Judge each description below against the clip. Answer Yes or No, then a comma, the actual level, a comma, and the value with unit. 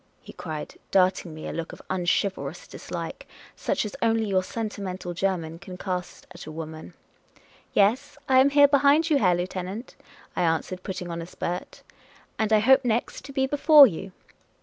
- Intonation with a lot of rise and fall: Yes, wide, 6.6 semitones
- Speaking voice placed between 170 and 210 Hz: Yes, high, 190 Hz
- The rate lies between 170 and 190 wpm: Yes, average, 185 wpm